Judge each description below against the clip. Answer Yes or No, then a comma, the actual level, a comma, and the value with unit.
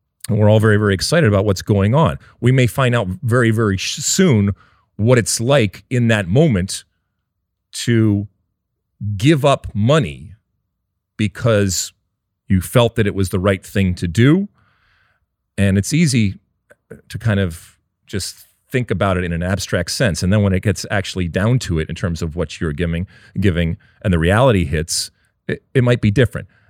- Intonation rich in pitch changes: No, average, 3.9 semitones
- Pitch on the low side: Yes, low, 100 Hz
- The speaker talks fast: No, average, 175 wpm